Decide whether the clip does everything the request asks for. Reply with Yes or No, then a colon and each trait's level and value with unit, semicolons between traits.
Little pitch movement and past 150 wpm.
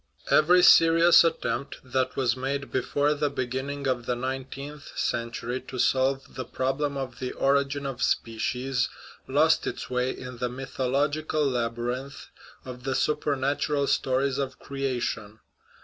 No: narrow, 1.9 semitones; slow, 135 wpm